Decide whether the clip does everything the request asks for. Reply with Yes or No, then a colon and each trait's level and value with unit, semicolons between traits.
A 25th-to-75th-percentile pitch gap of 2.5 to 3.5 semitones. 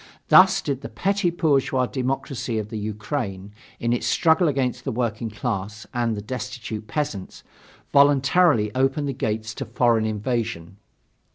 No: average, 4.3 semitones